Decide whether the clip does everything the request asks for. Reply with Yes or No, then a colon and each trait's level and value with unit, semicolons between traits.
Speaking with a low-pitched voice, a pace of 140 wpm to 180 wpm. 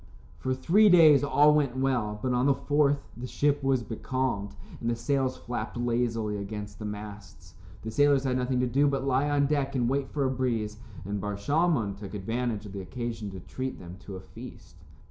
No: low, 125 Hz; fast, 205 wpm